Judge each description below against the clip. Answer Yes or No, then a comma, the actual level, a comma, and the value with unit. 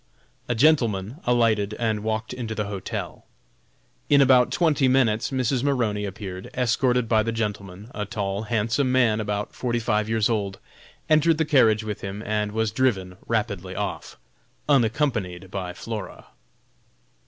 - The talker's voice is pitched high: No, low, 110 Hz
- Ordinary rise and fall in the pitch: Yes, average, 3.3 semitones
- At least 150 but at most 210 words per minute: No, average, 140 wpm